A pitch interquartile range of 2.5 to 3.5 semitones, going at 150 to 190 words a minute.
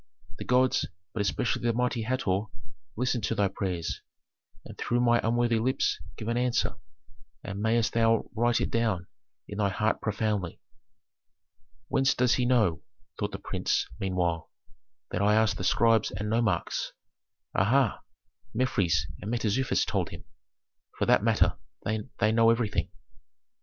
No: average, 3.2 semitones; average, 140 wpm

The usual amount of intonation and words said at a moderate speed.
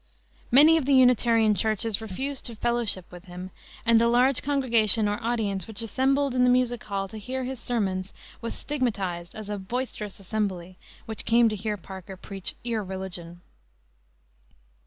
Yes: average, 4.1 semitones; average, 155 wpm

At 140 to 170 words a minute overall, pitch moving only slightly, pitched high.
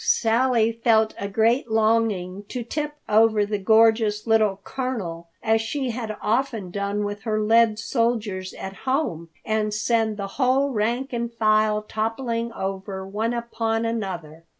Yes: average, 145 wpm; narrow, 2.1 semitones; high, 220 Hz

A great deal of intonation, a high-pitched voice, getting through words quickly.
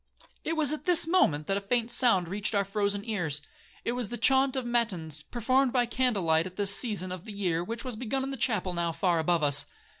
Yes: wide, 5.8 semitones; high, 210 Hz; fast, 220 wpm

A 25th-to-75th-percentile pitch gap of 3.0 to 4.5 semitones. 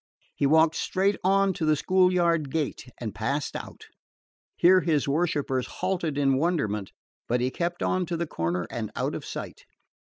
No: average, 5.0 semitones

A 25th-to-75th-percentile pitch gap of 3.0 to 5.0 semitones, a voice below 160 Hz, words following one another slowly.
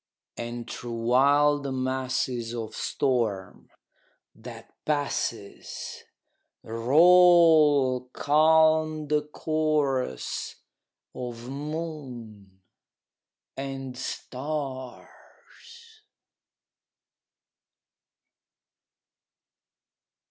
Yes: average, 4.0 semitones; low, 135 Hz; slow, 45 wpm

